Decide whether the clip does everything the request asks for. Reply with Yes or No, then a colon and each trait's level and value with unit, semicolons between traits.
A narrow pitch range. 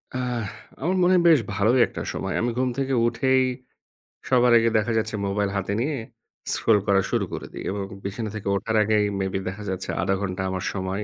No: average, 4.3 semitones